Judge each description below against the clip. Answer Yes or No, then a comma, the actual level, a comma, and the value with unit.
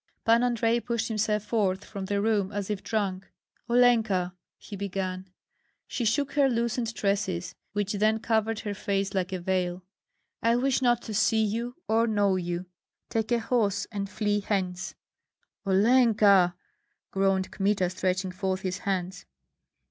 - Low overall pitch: No, high, 205 Hz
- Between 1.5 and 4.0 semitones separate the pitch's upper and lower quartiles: Yes, average, 3.0 semitones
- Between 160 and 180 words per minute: No, average, 150 wpm